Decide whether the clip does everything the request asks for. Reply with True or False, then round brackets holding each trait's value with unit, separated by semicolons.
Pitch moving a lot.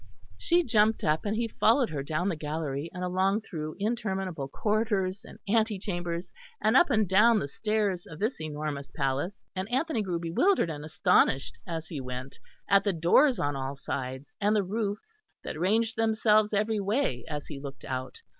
True (6.1 semitones)